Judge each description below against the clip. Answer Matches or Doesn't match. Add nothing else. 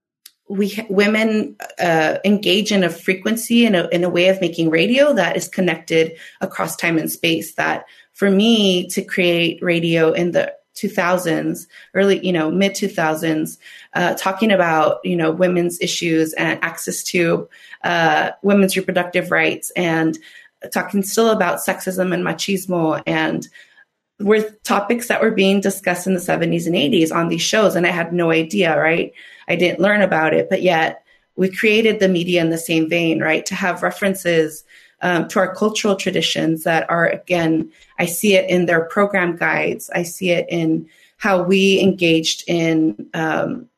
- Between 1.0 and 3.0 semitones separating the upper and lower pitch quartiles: Matches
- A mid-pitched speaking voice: Matches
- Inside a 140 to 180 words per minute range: Matches